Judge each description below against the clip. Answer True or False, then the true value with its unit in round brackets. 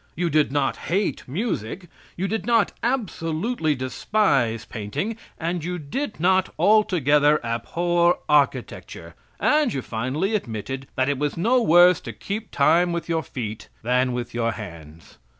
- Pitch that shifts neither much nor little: False (6.7 semitones)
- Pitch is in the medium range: True (160 Hz)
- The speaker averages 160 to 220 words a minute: False (145 wpm)